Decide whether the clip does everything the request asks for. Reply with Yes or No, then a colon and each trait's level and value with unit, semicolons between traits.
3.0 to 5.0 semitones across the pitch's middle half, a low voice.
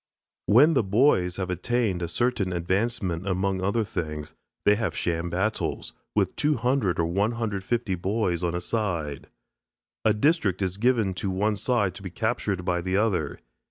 Yes: average, 4.1 semitones; low, 100 Hz